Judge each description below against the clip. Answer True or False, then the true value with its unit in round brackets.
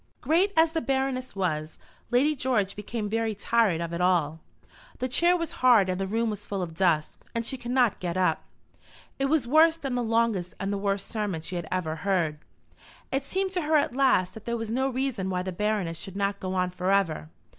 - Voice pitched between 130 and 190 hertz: False (210 Hz)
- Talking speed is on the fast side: True (220 wpm)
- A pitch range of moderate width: False (5.9 semitones)